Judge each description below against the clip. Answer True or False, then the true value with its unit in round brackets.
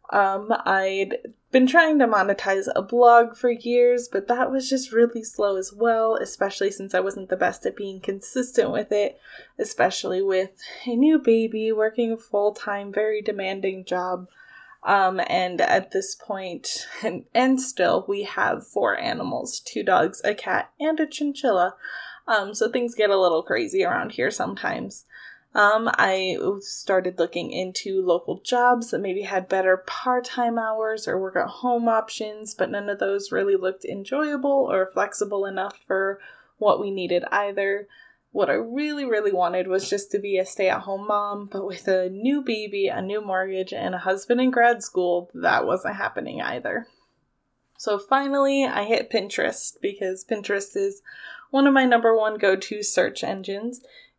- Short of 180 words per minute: True (170 wpm)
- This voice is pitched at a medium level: False (205 Hz)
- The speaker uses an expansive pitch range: False (3.9 semitones)